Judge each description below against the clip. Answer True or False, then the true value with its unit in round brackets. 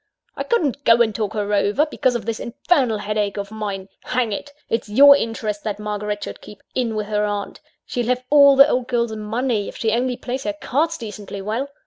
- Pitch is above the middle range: True (225 Hz)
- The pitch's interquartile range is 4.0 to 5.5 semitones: False (3.4 semitones)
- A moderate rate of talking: False (210 wpm)